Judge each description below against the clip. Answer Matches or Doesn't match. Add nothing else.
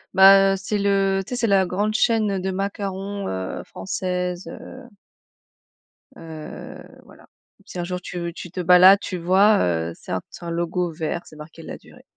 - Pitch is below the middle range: Doesn't match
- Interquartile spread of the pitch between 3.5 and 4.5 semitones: Doesn't match